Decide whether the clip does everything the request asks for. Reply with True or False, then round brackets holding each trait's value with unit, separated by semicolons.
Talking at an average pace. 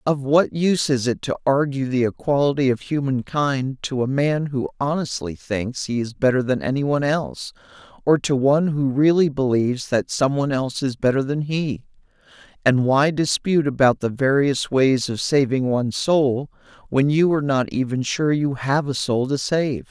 True (185 wpm)